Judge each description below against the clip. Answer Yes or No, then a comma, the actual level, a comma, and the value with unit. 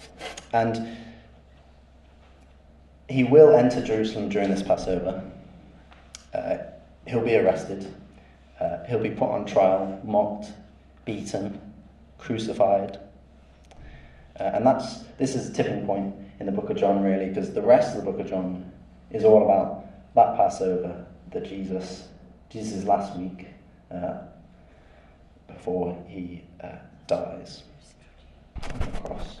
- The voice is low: Yes, very low, 95 Hz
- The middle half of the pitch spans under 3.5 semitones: No, average, 4.6 semitones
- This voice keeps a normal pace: No, slow, 125 wpm